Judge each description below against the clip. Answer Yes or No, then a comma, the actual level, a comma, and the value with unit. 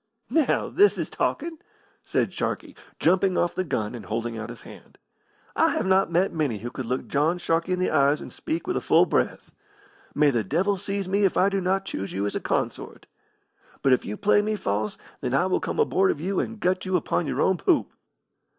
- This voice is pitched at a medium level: Yes, medium, 180 Hz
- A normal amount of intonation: No, wide, 6.9 semitones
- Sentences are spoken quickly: Yes, fast, 220 wpm